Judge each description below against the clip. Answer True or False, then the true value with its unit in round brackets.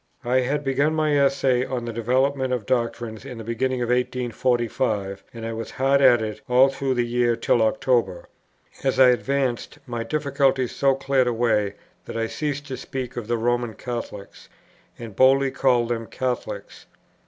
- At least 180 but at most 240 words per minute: False (170 wpm)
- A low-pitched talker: True (125 Hz)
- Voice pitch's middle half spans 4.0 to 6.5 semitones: False (2.5 semitones)